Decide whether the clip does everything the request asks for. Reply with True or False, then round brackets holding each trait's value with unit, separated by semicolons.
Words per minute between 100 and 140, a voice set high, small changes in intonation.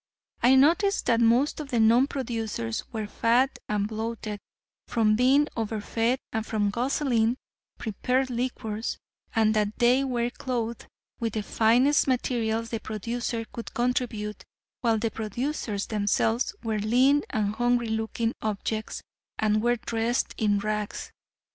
True (135 wpm; 230 Hz; 2.3 semitones)